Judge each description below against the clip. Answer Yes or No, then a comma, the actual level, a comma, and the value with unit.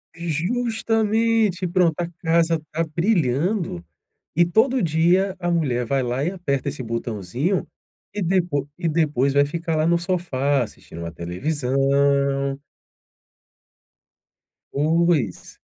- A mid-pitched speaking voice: Yes, medium, 160 Hz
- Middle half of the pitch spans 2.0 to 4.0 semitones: No, average, 4.4 semitones